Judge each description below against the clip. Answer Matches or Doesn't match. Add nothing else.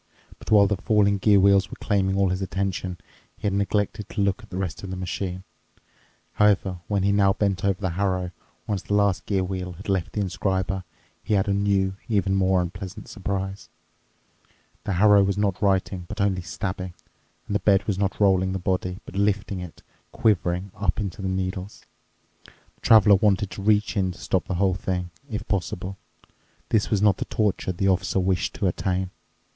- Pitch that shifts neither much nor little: Doesn't match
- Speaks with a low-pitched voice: Matches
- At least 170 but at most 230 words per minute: Matches